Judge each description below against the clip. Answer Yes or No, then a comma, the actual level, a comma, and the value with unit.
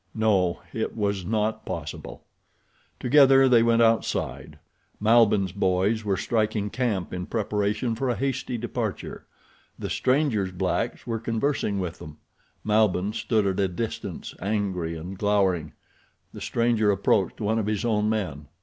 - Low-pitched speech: Yes, low, 105 Hz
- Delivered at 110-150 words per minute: Yes, average, 140 wpm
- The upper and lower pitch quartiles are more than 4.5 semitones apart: No, average, 3.2 semitones